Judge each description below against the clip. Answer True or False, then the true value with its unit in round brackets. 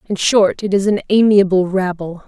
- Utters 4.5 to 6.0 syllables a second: True (4.8 syllables/s)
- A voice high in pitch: True (195 Hz)